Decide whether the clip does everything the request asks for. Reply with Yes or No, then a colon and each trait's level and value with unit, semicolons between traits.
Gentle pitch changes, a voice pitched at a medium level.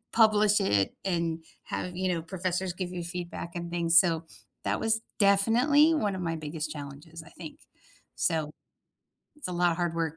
No: average, 3.2 semitones; medium, 175 Hz